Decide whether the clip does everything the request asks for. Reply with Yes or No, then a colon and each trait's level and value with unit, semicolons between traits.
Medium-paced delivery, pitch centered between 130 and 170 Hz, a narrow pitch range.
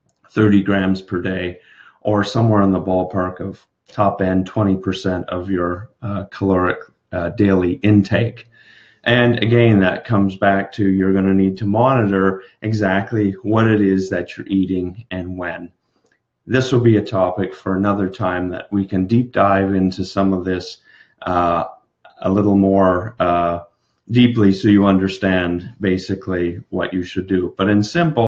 No: average, 160 wpm; very low, 95 Hz; narrow, 2.0 semitones